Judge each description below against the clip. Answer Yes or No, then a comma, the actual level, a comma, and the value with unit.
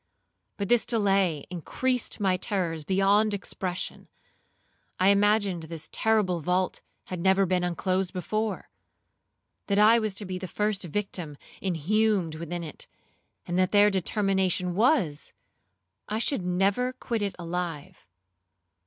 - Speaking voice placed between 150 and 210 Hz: Yes, high, 190 Hz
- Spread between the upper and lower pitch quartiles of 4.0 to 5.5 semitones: No, average, 2.9 semitones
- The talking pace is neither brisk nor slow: No, slow, 125 wpm